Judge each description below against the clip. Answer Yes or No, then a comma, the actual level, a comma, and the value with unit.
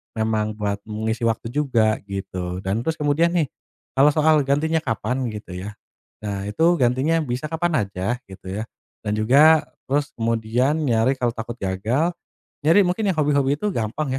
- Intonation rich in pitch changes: Yes, wide, 5.9 semitones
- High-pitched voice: No, low, 120 Hz